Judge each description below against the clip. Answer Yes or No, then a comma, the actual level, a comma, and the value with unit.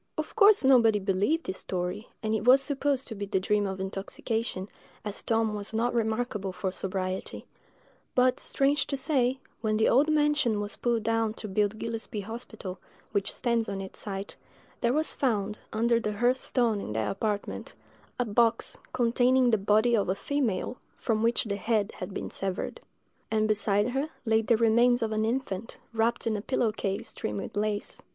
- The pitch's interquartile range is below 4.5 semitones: Yes, average, 3.2 semitones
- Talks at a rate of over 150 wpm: Yes, average, 180 wpm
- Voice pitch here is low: No, high, 220 Hz